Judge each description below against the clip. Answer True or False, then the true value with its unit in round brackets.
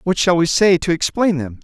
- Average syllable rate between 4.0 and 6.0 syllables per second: True (5.3 syllables/s)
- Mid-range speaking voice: True (170 Hz)